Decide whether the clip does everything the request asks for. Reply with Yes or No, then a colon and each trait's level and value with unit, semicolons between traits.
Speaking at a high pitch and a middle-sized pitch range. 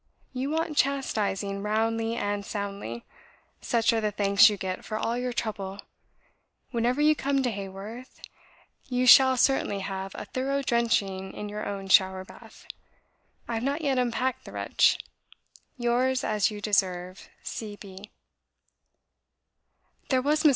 Yes: high, 220 Hz; average, 4.1 semitones